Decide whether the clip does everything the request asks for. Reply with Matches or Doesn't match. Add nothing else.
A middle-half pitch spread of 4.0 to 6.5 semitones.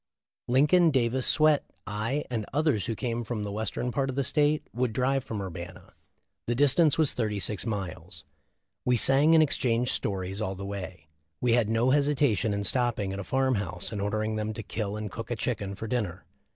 Matches